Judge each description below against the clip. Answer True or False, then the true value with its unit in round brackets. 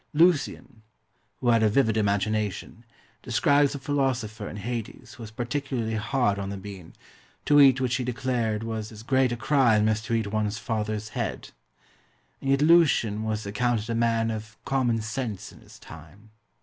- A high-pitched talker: False (115 Hz)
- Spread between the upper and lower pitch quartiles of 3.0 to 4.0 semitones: True (3.4 semitones)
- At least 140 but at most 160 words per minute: False (170 wpm)